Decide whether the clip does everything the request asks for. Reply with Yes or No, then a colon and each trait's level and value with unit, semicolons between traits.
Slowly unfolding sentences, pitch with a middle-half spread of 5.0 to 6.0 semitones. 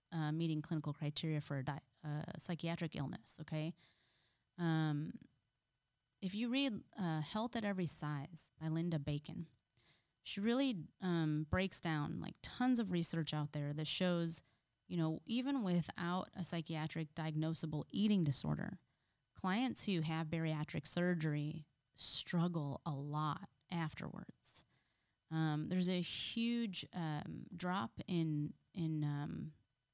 No: slow, 130 wpm; average, 3.0 semitones